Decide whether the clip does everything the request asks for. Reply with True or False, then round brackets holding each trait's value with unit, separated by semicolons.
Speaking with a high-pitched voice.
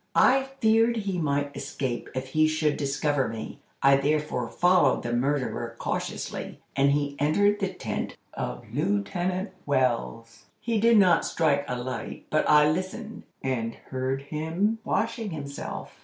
False (145 Hz)